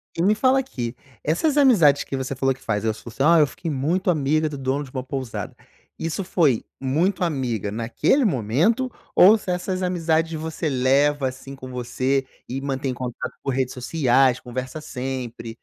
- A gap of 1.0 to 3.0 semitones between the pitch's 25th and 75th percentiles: No, average, 4.5 semitones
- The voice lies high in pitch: No, low, 135 Hz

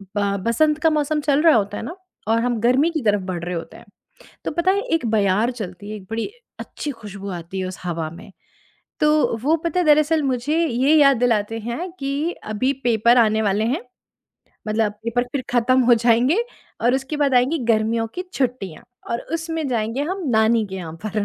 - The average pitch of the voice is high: Yes, high, 240 Hz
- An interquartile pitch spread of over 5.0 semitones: Yes, wide, 5.5 semitones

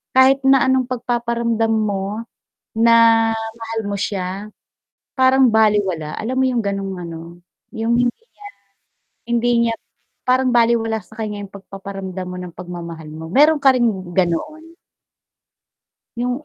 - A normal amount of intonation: Yes, average, 3.9 semitones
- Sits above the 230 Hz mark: No, high, 225 Hz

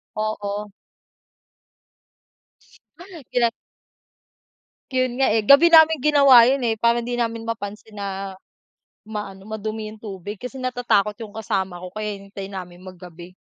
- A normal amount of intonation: Yes, average, 3.5 semitones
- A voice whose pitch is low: No, high, 215 Hz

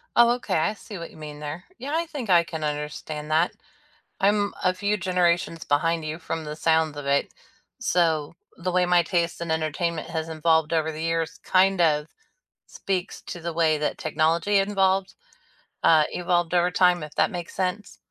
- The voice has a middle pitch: Yes, medium, 170 Hz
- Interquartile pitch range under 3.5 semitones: Yes, narrow, 2.6 semitones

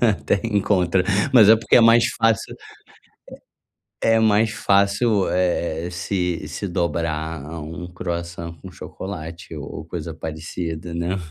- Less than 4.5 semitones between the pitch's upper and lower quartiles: Yes, average, 3.6 semitones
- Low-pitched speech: Yes, very low, 90 Hz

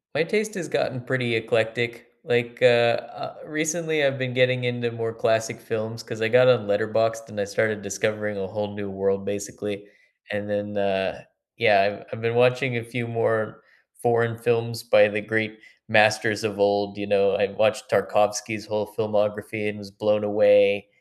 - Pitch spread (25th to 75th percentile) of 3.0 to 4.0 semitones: No, narrow, 2.4 semitones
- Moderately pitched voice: No, low, 110 Hz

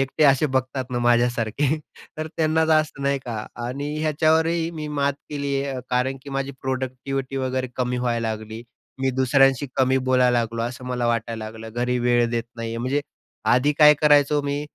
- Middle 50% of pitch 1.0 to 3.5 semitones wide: Yes, average, 2.7 semitones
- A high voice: No, low, 130 Hz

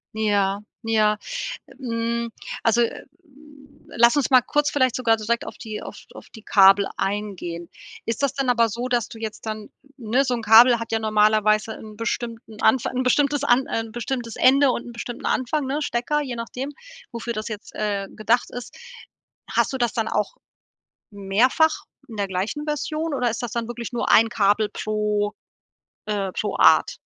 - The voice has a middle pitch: No, high, 230 Hz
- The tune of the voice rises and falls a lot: No, average, 2.8 semitones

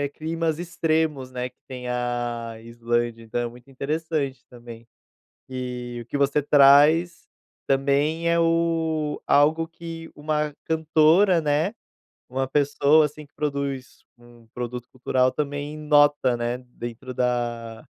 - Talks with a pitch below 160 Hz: Yes, medium, 140 Hz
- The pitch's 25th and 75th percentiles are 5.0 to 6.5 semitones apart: No, average, 4.1 semitones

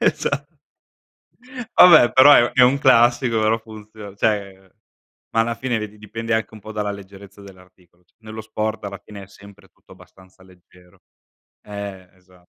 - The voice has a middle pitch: No, low, 105 Hz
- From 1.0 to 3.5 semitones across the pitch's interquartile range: Yes, average, 2.7 semitones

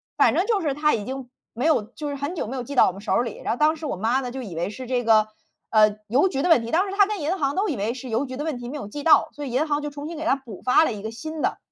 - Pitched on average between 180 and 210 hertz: No, very high, 270 Hz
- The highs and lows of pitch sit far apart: No, average, 4.9 semitones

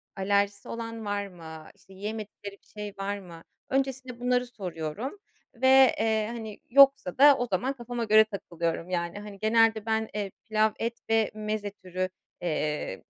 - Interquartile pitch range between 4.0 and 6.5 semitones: No, average, 3.2 semitones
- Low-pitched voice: No, high, 215 Hz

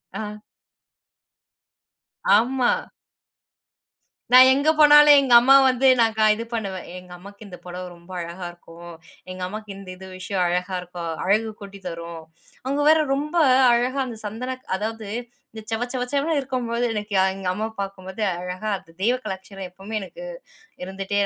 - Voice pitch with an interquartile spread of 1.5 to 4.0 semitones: No, average, 5.2 semitones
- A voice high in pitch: Yes, high, 205 Hz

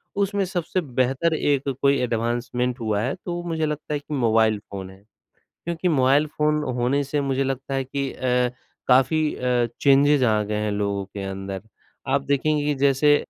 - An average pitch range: Yes, average, 3.8 semitones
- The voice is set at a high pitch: No, low, 135 Hz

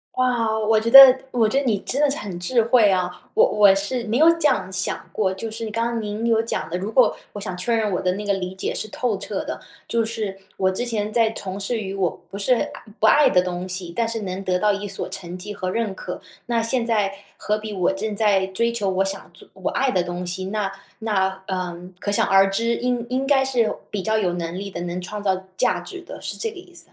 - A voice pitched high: Yes, high, 205 Hz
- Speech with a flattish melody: No, average, 3.5 semitones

